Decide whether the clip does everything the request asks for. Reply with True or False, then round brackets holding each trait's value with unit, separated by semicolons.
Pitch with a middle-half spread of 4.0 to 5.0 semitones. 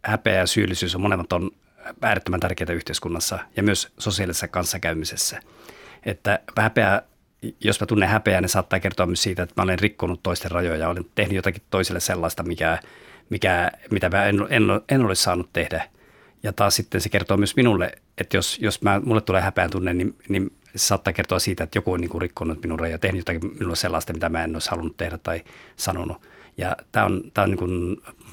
False (2.7 semitones)